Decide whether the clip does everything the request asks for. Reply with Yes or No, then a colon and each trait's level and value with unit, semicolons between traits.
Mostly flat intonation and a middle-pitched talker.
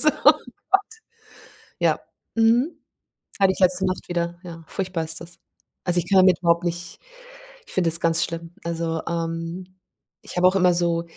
Yes: narrow, 1.9 semitones; medium, 175 Hz